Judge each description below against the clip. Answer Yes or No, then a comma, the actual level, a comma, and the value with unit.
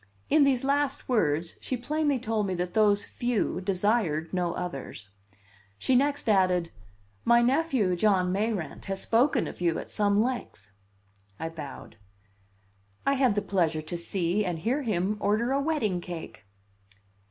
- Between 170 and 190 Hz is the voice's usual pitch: No, high, 205 Hz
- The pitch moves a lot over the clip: Yes, wide, 6.0 semitones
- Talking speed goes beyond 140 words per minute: Yes, average, 150 wpm